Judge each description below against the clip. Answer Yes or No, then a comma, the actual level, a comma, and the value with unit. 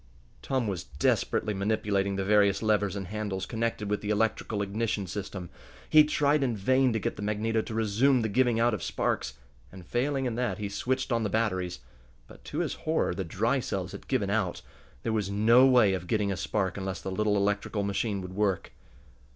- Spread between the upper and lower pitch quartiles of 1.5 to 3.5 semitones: Yes, average, 2.9 semitones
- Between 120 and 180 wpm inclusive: No, average, 200 wpm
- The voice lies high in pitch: No, low, 105 Hz